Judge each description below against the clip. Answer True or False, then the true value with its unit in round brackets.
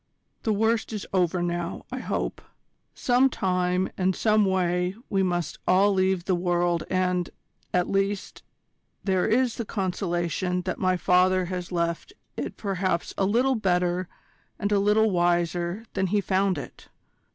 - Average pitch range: False (2.1 semitones)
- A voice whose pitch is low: False (185 Hz)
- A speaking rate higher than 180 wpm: False (150 wpm)